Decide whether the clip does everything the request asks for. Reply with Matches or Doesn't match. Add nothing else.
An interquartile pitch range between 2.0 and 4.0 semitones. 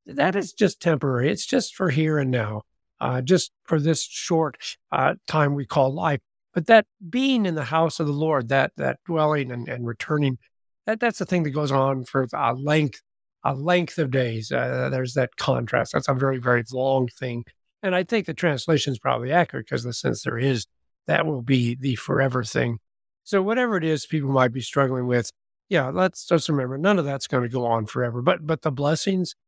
Doesn't match